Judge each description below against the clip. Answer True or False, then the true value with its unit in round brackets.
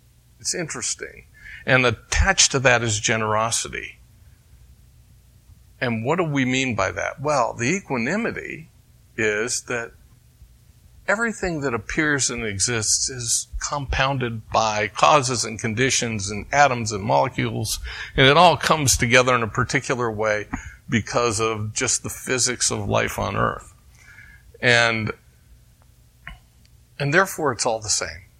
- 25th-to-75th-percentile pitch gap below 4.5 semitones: True (3.7 semitones)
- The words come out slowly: True (125 wpm)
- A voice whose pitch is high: False (120 Hz)